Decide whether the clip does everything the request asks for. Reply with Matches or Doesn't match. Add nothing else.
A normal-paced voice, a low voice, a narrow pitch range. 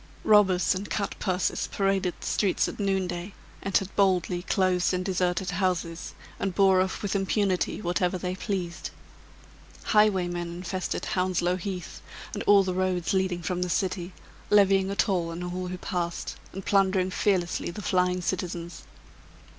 Doesn't match